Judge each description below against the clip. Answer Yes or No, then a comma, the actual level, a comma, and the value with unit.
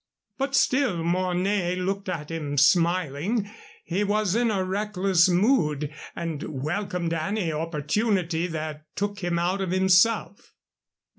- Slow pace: Yes, slow, 125 wpm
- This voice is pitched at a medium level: Yes, medium, 180 Hz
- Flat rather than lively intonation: No, average, 3.6 semitones